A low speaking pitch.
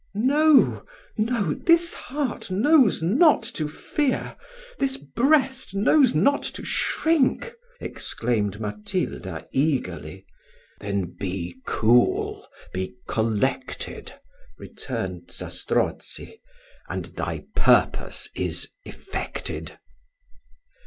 No: high, 190 Hz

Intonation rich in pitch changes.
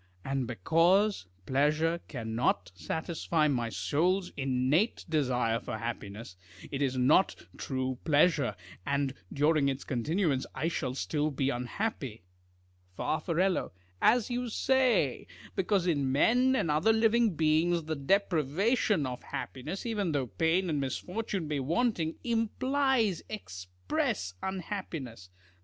Yes: wide, 6.8 semitones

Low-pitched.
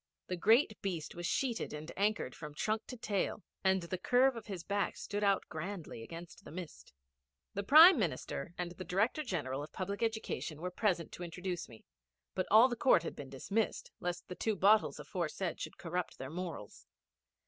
No: medium, 185 Hz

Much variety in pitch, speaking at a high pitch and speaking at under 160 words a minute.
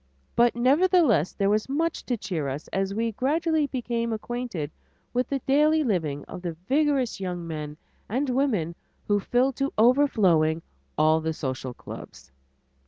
Yes: wide, 8.4 semitones; high, 230 Hz; average, 150 wpm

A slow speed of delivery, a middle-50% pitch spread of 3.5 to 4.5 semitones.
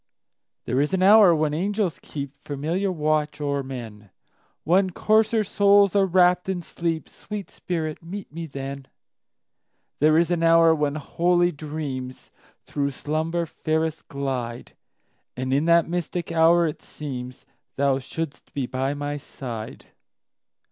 Yes: slow, 115 wpm; average, 3.8 semitones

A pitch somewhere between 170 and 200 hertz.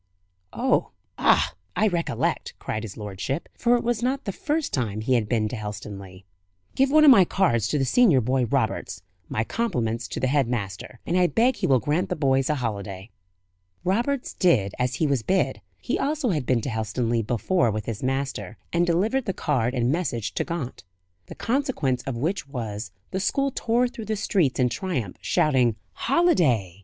No: low, 135 Hz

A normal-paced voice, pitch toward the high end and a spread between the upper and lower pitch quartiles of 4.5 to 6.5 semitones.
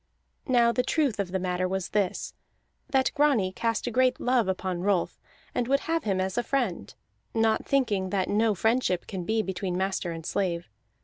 Yes: average, 185 wpm; high, 205 Hz; average, 4.8 semitones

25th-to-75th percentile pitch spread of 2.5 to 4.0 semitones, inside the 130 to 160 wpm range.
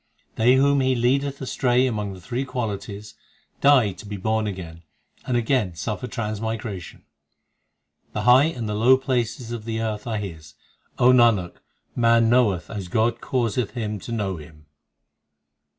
Yes: average, 3.4 semitones; average, 150 wpm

